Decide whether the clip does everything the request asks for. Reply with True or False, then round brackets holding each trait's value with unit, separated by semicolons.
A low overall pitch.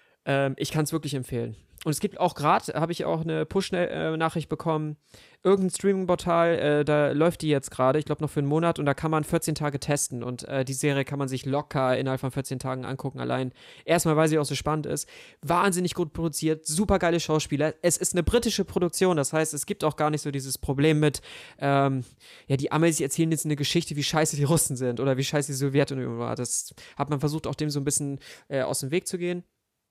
False (150 Hz)